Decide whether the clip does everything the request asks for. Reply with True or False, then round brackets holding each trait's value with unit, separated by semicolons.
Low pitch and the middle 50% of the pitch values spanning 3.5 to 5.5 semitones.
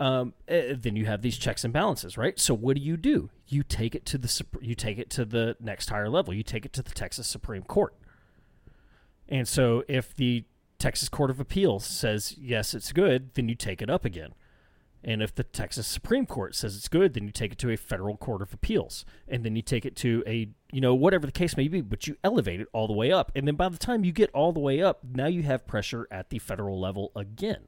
True (120 Hz; 4.3 semitones)